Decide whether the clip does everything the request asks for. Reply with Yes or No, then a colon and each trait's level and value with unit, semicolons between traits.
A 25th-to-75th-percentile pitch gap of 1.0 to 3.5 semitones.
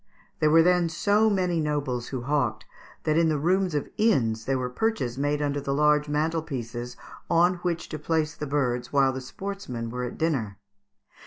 No: average, 4.7 semitones